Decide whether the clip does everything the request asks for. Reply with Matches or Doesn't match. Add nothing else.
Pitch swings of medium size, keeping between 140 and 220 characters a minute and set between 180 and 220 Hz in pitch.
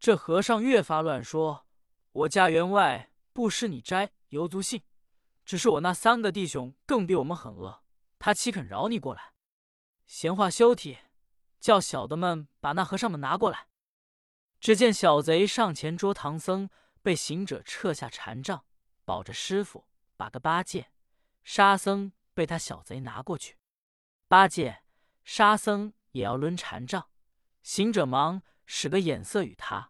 Matches